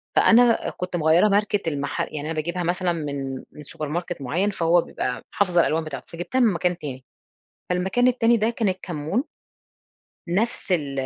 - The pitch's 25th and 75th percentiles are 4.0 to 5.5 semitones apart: Yes, average, 4.7 semitones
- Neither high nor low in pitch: Yes, medium, 175 Hz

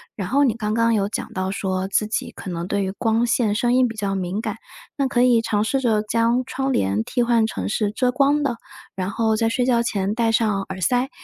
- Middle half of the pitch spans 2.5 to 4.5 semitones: Yes, average, 3.5 semitones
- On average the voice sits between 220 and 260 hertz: Yes, high, 225 Hz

